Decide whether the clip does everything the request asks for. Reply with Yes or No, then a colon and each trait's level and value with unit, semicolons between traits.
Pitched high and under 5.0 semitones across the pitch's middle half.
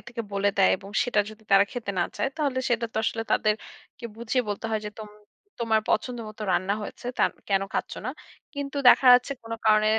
Yes: high, 220 Hz; average, 2.9 semitones